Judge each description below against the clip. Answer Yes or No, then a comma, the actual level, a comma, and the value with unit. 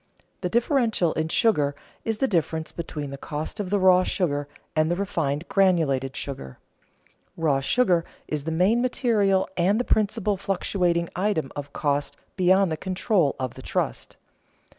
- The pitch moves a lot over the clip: No, average, 4.9 semitones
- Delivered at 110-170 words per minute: Yes, average, 155 wpm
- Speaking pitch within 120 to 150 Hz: No, medium, 175 Hz